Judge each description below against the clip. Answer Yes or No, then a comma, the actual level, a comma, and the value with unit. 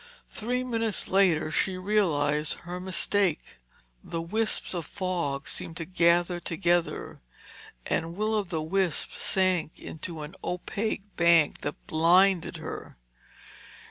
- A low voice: No, medium, 175 Hz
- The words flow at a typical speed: No, slow, 120 wpm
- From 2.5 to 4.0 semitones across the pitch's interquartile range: Yes, average, 3.1 semitones